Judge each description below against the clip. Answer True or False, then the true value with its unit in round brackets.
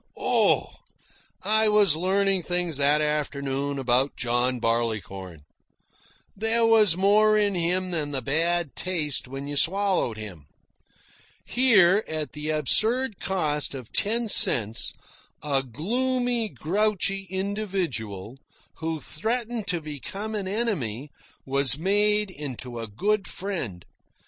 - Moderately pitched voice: True (170 Hz)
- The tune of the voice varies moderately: False (7.2 semitones)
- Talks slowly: True (115 wpm)